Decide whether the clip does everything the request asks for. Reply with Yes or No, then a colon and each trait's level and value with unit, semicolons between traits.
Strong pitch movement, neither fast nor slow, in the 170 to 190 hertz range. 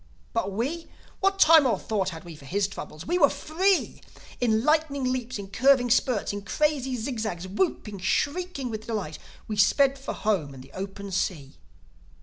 No: wide, 6.3 semitones; average, 165 wpm; high, 225 Hz